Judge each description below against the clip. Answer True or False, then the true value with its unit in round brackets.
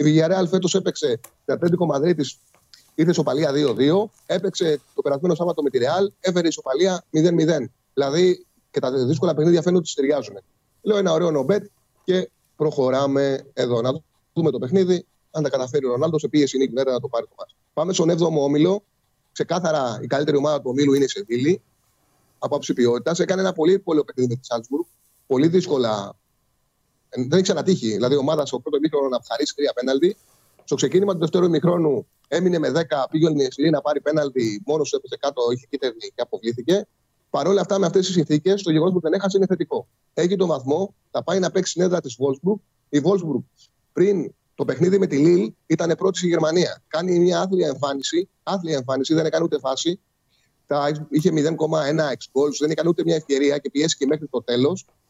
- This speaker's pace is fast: True (190 wpm)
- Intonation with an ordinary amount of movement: True (4.5 semitones)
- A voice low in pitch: False (160 Hz)